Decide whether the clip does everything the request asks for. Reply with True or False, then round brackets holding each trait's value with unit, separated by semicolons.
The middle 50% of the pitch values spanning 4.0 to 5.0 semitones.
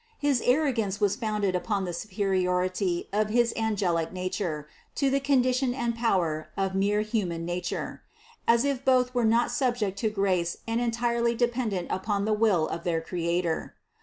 True (4.6 semitones)